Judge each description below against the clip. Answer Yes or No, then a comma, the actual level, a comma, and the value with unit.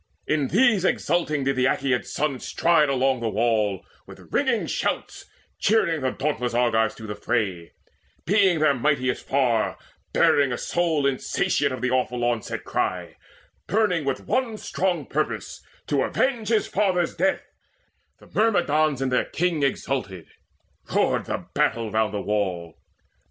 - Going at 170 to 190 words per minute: No, average, 145 wpm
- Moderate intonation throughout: No, wide, 6.2 semitones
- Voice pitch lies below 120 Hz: No, low, 135 Hz